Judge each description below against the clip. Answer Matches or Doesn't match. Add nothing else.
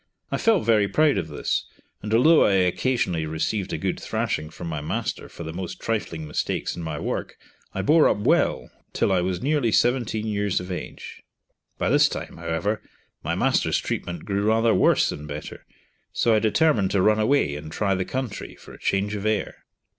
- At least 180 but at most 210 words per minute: Matches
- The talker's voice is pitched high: Doesn't match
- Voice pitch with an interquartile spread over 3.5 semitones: Matches